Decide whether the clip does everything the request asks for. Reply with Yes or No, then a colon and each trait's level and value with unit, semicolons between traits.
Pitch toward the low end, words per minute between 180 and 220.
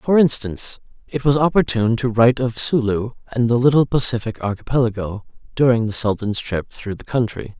No: low, 120 Hz; average, 165 wpm